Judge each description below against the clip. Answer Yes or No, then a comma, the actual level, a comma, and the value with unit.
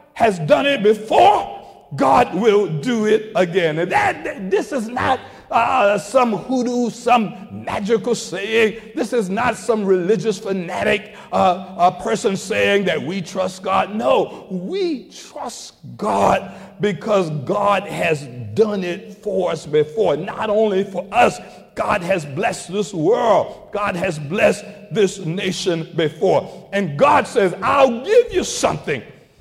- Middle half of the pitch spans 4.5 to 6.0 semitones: No, average, 3.4 semitones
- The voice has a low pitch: No, high, 205 Hz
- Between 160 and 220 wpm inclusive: No, average, 140 wpm